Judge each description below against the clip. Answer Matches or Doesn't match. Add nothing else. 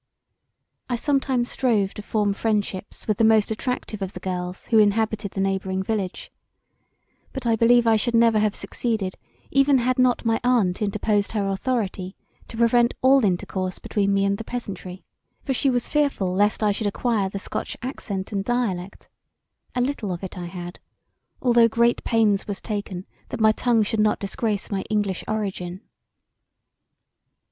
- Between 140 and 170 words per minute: Matches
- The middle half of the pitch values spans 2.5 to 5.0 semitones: Matches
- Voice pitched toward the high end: Matches